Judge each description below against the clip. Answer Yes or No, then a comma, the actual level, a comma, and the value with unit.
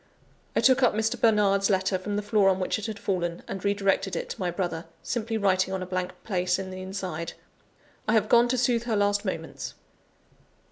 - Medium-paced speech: No, fast, 215 wpm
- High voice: Yes, high, 195 Hz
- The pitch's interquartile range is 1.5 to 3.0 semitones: Yes, narrow, 2.6 semitones